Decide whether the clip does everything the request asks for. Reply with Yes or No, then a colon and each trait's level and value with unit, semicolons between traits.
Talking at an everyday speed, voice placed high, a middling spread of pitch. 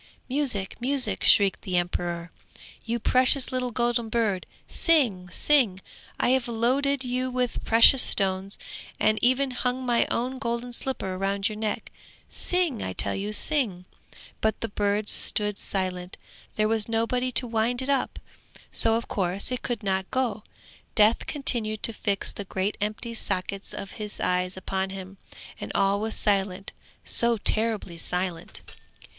Yes: average, 150 wpm; high, 220 Hz; average, 4.2 semitones